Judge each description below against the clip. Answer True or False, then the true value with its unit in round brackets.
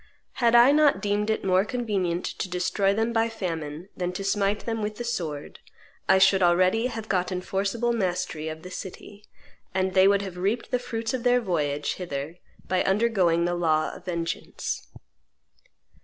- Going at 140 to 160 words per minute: False (170 wpm)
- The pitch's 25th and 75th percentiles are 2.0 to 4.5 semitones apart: True (4.1 semitones)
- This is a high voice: True (195 Hz)